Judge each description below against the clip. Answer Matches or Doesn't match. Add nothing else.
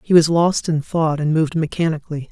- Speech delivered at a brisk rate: Matches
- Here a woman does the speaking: Doesn't match